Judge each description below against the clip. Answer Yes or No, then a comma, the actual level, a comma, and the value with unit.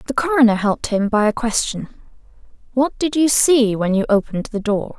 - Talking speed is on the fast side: No, average, 195 wpm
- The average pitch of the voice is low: No, high, 235 Hz